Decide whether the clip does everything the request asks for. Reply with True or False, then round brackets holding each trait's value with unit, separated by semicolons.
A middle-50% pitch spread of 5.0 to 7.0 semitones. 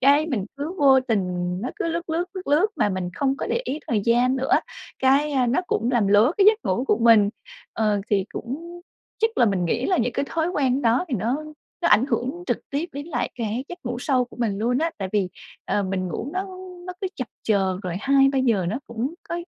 True (5.6 semitones)